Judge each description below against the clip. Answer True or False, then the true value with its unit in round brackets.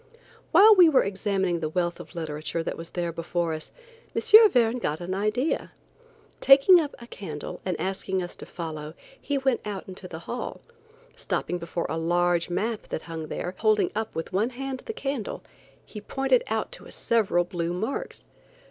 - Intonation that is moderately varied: False (6.4 semitones)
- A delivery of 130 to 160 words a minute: False (180 wpm)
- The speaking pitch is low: False (190 Hz)